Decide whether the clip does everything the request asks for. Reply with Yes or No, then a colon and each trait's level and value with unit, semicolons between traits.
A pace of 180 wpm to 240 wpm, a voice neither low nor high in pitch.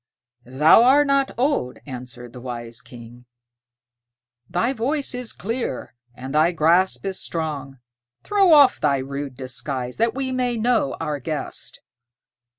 No: slow, 135 wpm; medium, 160 Hz